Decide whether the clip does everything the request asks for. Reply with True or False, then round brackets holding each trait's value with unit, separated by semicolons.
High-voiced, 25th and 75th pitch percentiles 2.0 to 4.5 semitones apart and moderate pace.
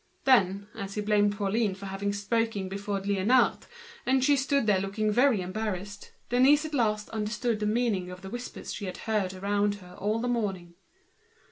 True (205 Hz; 3.0 semitones; 165 wpm)